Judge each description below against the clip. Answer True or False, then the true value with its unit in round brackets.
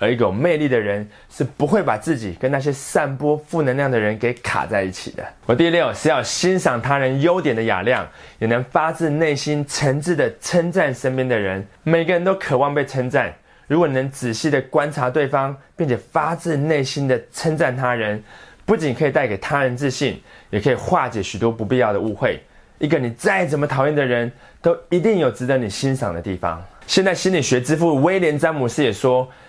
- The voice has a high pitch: False (140 Hz)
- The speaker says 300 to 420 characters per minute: True (305 characters per minute)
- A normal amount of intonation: True (4.9 semitones)